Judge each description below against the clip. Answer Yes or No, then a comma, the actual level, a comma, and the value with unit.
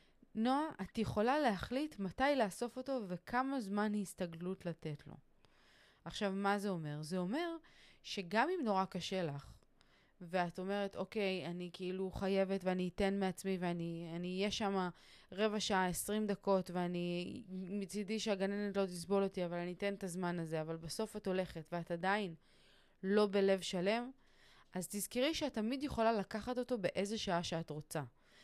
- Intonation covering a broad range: No, average, 3.0 semitones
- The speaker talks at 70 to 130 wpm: No, fast, 150 wpm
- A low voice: No, high, 195 Hz